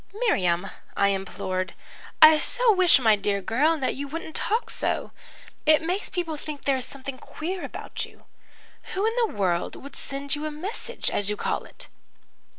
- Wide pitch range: Yes, wide, 8.9 semitones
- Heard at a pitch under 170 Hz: No, very high, 290 Hz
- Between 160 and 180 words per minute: Yes, average, 175 wpm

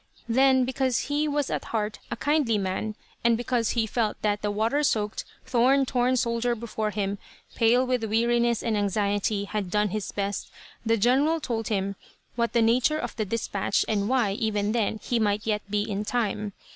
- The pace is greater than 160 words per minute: Yes, average, 185 wpm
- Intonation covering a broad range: No, average, 2.9 semitones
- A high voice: Yes, high, 225 Hz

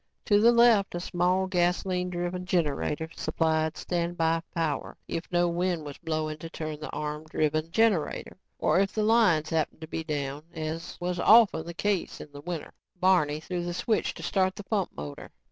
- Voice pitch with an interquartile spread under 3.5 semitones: Yes, average, 2.9 semitones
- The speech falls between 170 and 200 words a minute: Yes, average, 180 wpm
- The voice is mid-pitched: Yes, medium, 170 Hz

